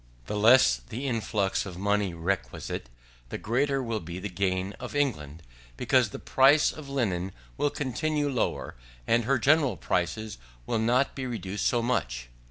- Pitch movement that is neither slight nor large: No, wide, 6.1 semitones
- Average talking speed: Yes, average, 160 wpm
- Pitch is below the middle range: Yes, low, 110 Hz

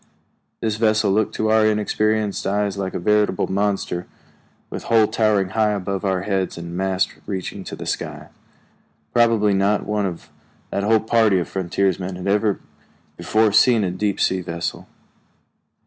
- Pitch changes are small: Yes, narrow, 2.3 semitones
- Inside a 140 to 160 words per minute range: Yes, average, 155 wpm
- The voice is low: Yes, low, 100 Hz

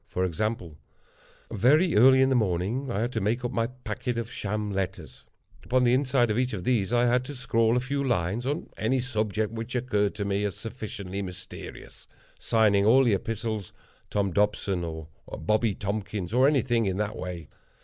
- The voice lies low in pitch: Yes, low, 110 Hz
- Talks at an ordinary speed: Yes, average, 180 wpm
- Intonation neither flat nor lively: Yes, average, 3.8 semitones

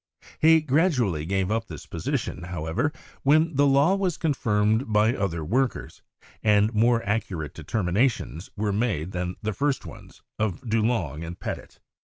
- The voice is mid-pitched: No, low, 110 Hz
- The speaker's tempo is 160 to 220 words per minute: No, average, 145 wpm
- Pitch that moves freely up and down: Yes, wide, 6.7 semitones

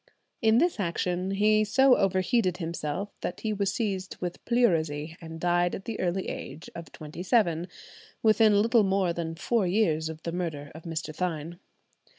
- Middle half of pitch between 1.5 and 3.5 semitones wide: No, average, 4.3 semitones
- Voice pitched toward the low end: No, medium, 180 Hz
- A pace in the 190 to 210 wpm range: No, average, 165 wpm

